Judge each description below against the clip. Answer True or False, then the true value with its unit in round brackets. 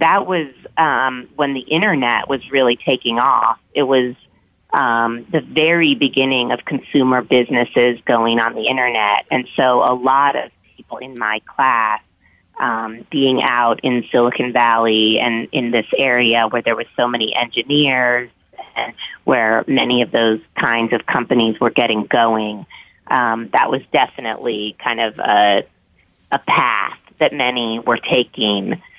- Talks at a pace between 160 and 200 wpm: False (150 wpm)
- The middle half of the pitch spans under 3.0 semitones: True (2.4 semitones)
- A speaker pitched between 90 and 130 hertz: True (120 Hz)